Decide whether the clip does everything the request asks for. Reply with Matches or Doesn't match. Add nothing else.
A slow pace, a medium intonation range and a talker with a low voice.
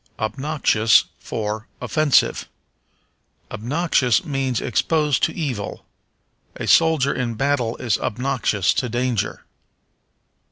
Matches